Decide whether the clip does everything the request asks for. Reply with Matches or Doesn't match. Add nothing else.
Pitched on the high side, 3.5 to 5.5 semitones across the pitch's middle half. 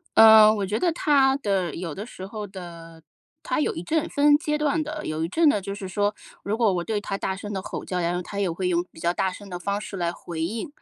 Matches